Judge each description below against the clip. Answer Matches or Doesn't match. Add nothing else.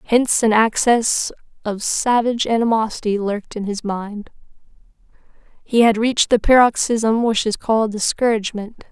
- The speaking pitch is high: Matches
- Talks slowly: Matches